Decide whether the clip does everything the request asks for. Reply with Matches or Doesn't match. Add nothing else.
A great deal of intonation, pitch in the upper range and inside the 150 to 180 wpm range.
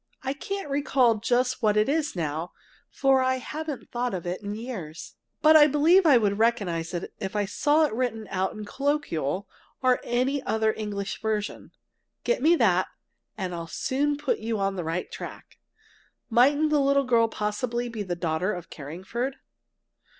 Matches